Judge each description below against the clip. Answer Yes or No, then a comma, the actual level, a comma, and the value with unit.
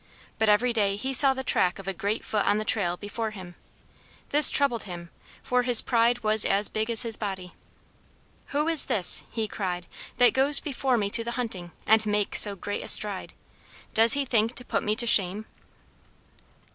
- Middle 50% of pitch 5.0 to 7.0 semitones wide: No, average, 3.5 semitones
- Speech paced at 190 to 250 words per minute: Yes, average, 195 wpm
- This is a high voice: Yes, high, 220 Hz